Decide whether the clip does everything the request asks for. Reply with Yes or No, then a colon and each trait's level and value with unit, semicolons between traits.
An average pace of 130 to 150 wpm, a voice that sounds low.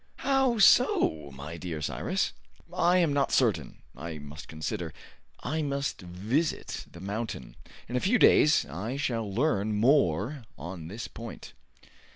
Yes: average, 140 wpm; low, 110 Hz